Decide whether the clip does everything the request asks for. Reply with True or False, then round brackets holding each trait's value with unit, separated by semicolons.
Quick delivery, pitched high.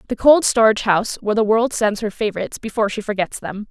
True (225 wpm; 215 Hz)